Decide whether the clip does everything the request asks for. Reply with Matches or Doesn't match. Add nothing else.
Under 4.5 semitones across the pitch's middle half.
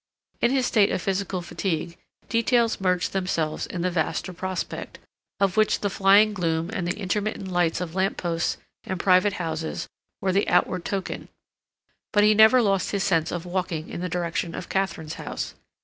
Matches